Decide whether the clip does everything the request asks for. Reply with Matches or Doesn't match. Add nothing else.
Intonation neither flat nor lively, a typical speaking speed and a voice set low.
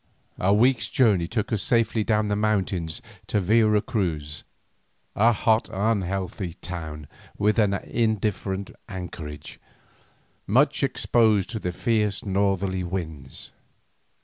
Doesn't match